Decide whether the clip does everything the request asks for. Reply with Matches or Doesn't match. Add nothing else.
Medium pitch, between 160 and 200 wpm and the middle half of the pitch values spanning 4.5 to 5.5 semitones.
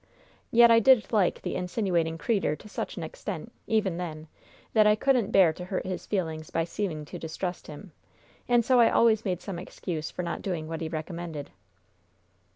Matches